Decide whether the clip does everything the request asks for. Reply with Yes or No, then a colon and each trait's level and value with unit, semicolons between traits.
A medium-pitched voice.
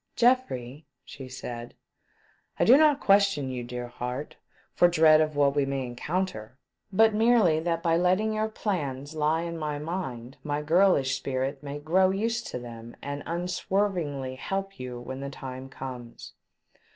Yes: medium, 150 Hz